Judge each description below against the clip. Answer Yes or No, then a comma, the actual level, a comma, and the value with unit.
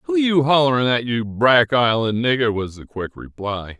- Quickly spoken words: No, average, 190 wpm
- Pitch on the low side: Yes, low, 115 Hz